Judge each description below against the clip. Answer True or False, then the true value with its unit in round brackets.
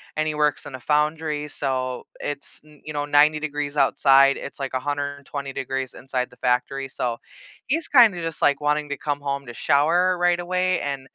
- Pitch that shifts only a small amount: True (2.0 semitones)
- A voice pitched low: False (145 Hz)